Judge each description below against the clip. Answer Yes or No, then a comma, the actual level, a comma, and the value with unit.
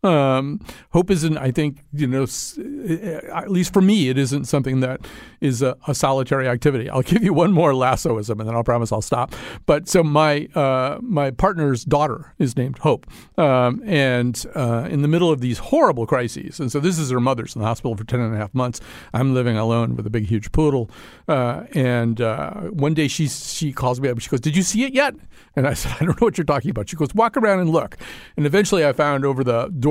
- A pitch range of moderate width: Yes, average, 4.5 semitones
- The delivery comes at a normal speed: No, fast, 235 wpm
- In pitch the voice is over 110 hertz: Yes, medium, 140 Hz